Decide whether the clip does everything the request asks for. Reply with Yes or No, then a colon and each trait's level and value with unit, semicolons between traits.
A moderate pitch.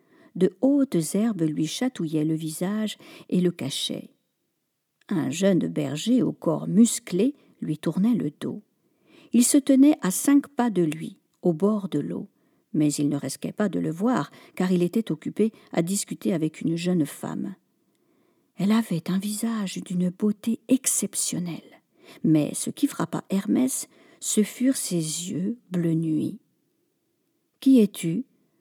No: high, 210 Hz